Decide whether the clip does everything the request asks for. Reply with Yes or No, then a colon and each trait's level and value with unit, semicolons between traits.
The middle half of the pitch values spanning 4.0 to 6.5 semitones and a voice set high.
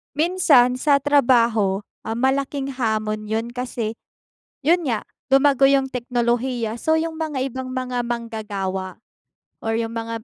No: average, 3.3 semitones; high, 245 Hz